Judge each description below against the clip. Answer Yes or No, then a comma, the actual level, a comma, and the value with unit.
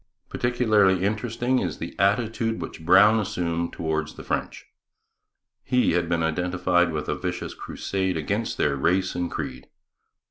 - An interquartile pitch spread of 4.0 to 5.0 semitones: Yes, average, 4.4 semitones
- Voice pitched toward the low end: Yes, very low, 90 Hz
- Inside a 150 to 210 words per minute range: No, average, 140 wpm